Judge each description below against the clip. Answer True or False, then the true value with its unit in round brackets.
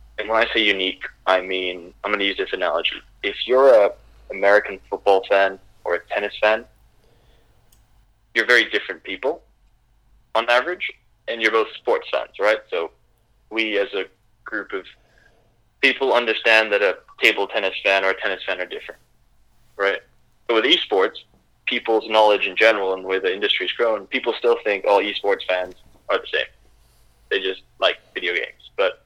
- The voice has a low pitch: True (110 Hz)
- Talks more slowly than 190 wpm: True (170 wpm)